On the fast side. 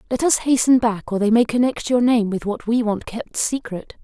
Yes: fast, 240 wpm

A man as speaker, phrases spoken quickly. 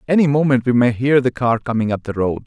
Yes: male; fast, 270 wpm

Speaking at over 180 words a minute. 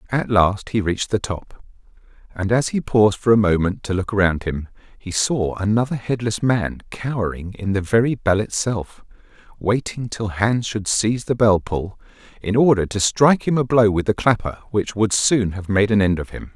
Yes: average, 200 wpm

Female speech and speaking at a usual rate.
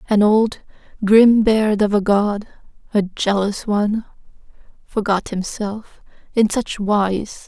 No: female; slow, 120 wpm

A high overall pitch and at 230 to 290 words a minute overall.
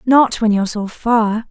No: high, 225 Hz; average, 200 wpm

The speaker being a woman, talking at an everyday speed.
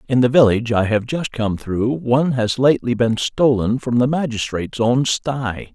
No: male; average, 190 wpm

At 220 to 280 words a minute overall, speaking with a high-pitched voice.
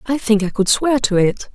Yes: fast, 270 wpm; high, 225 Hz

